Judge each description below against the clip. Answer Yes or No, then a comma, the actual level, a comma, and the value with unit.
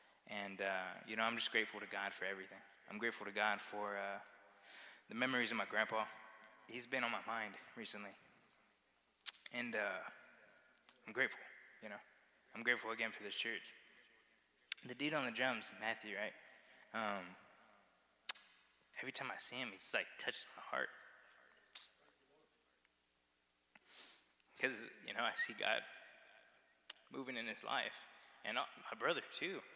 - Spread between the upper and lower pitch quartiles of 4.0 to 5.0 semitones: No, average, 2.9 semitones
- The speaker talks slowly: No, average, 145 wpm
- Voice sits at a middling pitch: No, low, 110 Hz